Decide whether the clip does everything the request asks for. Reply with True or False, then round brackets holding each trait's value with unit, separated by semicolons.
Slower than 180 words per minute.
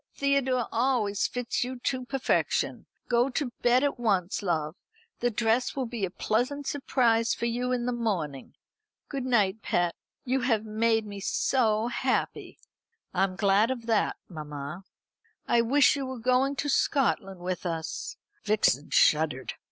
True (150 wpm)